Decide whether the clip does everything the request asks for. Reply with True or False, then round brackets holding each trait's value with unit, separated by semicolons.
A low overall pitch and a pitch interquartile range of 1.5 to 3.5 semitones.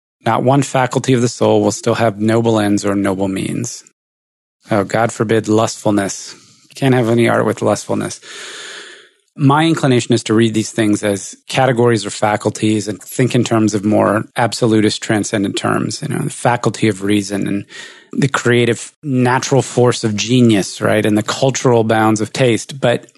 True (115 Hz; 2.8 semitones)